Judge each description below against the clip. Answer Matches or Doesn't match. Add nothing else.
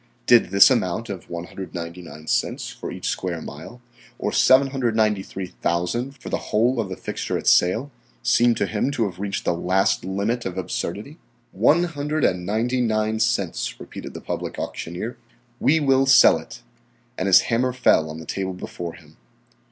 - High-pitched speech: Doesn't match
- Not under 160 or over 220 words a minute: Matches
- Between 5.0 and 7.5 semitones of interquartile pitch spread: Matches